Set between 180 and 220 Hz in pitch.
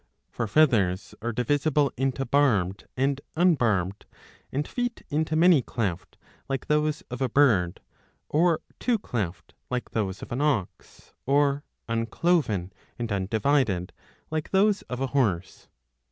No: low, 130 Hz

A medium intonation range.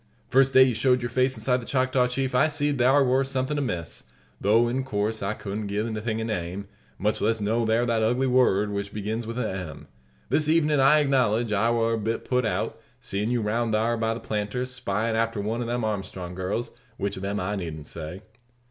Yes: average, 3.4 semitones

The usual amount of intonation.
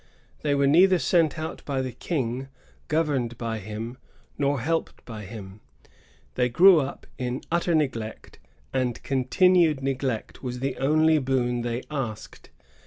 Yes: average, 4.3 semitones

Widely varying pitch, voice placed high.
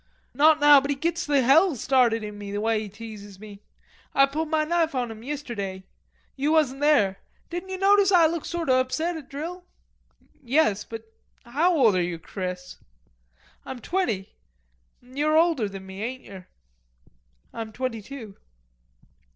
Yes: wide, 6.7 semitones; very high, 260 Hz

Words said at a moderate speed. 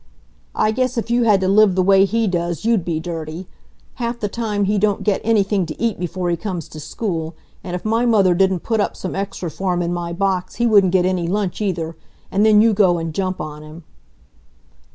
No: fast, 225 wpm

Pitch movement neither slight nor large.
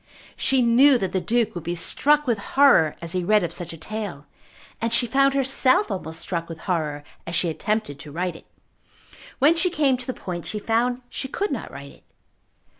No: wide, 7.1 semitones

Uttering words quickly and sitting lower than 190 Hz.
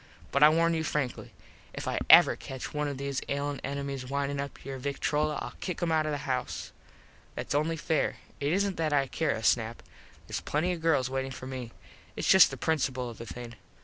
Yes: fast, 210 wpm; medium, 140 Hz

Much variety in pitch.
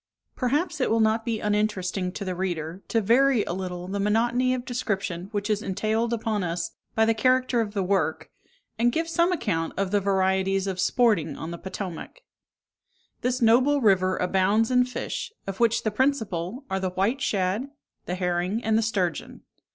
No: average, 4.2 semitones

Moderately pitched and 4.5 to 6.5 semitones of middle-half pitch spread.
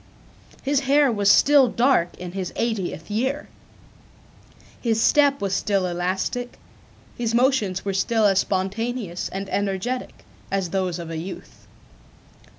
No: high, 205 Hz; average, 4.8 semitones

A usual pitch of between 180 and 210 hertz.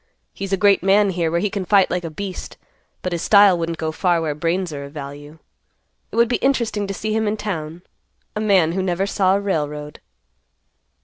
Yes: medium, 185 Hz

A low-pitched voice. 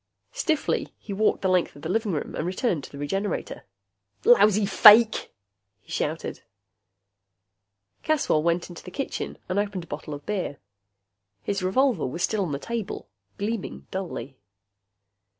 No: high, 195 Hz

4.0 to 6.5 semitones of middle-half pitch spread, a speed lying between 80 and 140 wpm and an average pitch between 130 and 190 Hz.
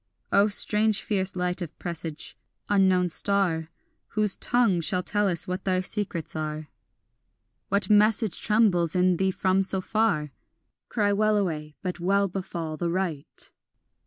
No: average, 3.0 semitones; slow, 135 wpm; medium, 185 Hz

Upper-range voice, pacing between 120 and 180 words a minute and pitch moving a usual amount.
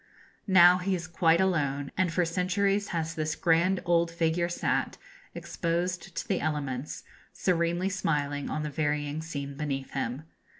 No: medium, 165 Hz; average, 145 wpm; average, 3.3 semitones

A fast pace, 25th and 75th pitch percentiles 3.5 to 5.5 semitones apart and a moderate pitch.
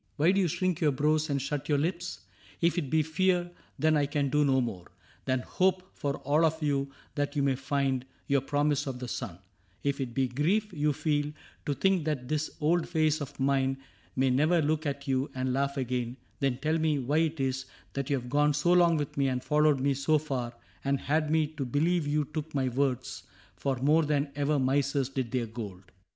No: fast, 215 wpm; average, 2.7 semitones; medium, 145 Hz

